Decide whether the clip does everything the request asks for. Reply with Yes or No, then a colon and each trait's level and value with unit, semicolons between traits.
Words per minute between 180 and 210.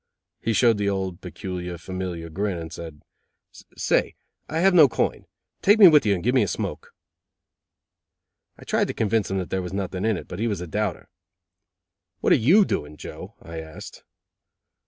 Yes: average, 185 wpm